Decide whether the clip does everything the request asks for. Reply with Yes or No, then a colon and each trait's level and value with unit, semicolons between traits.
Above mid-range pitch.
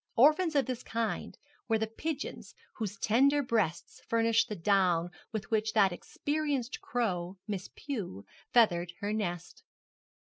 Yes: high, 220 Hz